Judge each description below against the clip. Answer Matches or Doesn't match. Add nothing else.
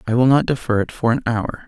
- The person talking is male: Matches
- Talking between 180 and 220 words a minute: Doesn't match